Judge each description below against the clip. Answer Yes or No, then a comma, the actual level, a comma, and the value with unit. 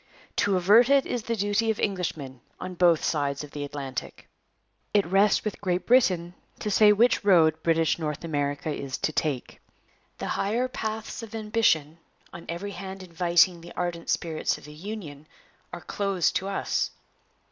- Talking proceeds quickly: No, average, 165 wpm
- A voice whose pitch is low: No, medium, 180 Hz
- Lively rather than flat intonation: No, average, 4.7 semitones